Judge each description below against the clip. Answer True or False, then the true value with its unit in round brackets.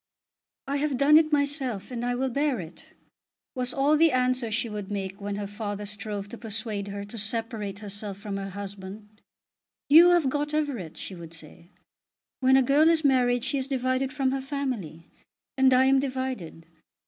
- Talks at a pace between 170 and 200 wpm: True (185 wpm)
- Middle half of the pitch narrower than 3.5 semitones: False (5.0 semitones)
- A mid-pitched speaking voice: False (245 Hz)